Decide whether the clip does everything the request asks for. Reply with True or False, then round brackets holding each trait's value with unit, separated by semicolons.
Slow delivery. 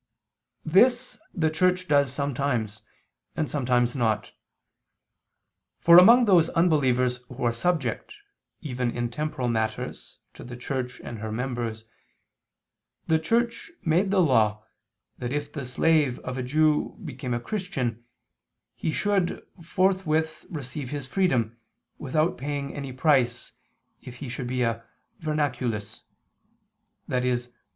True (125 wpm)